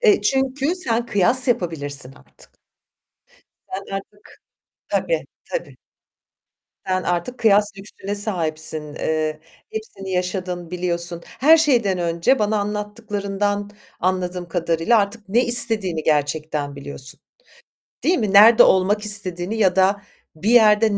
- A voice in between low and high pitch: No, high, 195 Hz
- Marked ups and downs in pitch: No, average, 4.2 semitones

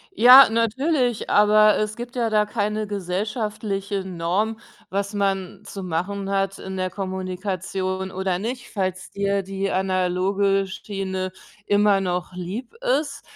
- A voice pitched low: No, high, 195 Hz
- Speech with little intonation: Yes, narrow, 2.2 semitones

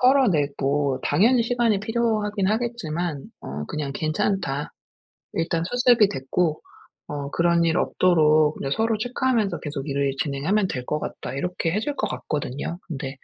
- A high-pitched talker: No, medium, 170 Hz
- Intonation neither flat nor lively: No, wide, 7.1 semitones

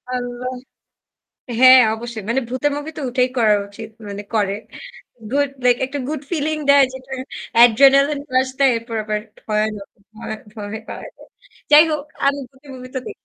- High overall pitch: Yes, very high, 255 Hz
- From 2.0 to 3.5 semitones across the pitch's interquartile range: No, average, 4.0 semitones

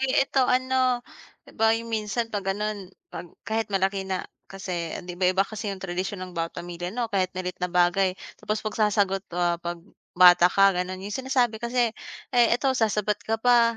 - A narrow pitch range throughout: No, average, 3.8 semitones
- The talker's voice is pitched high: Yes, high, 200 Hz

